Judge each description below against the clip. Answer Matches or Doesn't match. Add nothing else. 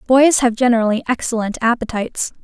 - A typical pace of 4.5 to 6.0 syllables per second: Doesn't match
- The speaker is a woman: Matches